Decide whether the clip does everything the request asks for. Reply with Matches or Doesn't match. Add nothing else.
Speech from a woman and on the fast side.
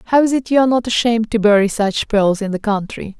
Matches